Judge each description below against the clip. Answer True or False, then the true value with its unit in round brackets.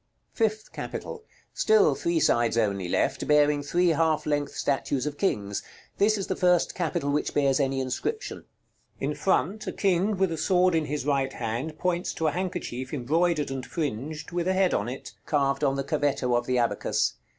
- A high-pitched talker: False (150 Hz)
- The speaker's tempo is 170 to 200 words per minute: True (185 wpm)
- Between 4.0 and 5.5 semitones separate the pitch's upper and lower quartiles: True (4.9 semitones)